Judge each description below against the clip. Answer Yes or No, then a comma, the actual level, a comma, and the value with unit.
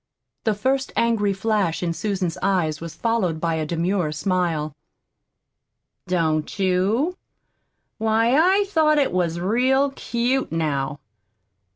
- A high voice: Yes, high, 195 Hz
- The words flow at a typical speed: No, slow, 115 wpm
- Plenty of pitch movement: Yes, wide, 6.1 semitones